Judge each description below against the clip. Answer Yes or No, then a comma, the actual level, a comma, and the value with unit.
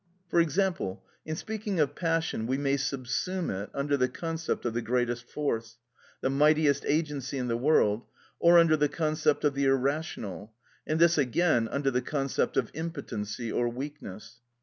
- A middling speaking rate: Yes, average, 165 wpm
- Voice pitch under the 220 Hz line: Yes, medium, 140 Hz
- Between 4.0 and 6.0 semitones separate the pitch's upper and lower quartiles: Yes, average, 4.5 semitones